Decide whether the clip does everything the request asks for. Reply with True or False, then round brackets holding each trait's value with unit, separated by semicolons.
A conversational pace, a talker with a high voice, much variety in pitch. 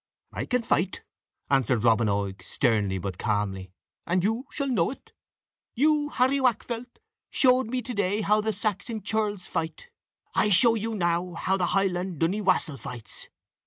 True (160 wpm; 195 Hz; 8.8 semitones)